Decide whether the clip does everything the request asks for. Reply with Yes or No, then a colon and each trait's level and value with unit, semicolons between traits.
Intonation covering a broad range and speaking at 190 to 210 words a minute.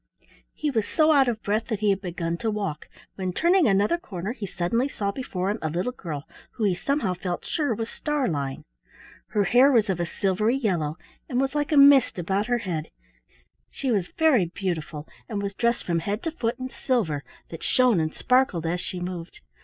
Yes: wide, 6.3 semitones; average, 200 wpm